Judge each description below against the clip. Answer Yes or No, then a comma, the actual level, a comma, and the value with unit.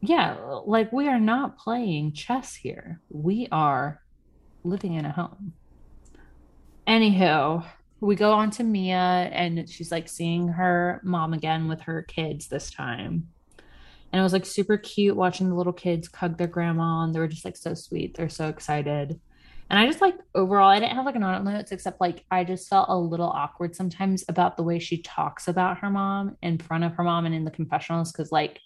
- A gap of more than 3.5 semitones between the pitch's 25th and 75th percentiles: No, average, 3.2 semitones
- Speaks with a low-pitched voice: No, medium, 175 Hz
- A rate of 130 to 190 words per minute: No, average, 200 wpm